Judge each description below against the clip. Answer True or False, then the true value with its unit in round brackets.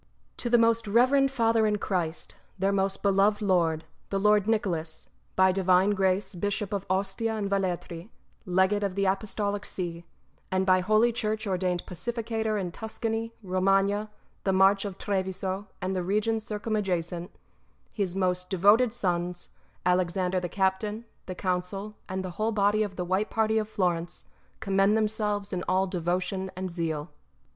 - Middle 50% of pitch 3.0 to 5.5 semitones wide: False (2.5 semitones)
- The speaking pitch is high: True (195 Hz)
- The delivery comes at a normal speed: True (150 wpm)